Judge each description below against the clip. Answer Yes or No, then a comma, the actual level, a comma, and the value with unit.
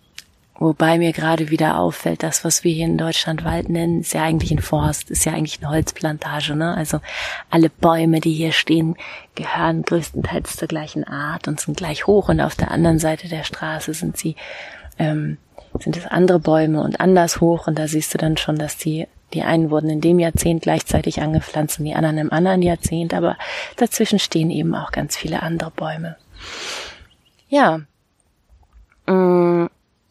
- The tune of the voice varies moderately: No, narrow, 1.4 semitones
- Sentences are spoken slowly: No, average, 175 wpm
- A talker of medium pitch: Yes, medium, 160 Hz